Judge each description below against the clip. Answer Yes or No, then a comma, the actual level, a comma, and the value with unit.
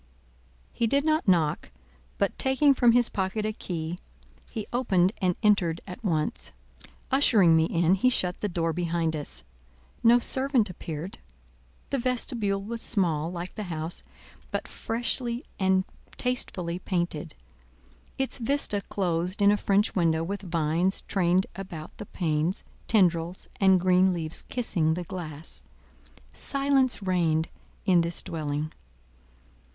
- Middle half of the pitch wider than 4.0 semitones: Yes, average, 5.0 semitones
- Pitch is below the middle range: No, medium, 185 Hz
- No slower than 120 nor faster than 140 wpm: Yes, slow, 135 wpm